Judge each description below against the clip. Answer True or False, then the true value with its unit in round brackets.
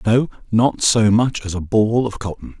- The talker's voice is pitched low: True (110 Hz)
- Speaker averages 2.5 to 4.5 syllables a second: True (4.4 syllables/s)